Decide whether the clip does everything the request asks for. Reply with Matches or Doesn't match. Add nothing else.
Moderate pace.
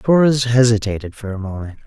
Matches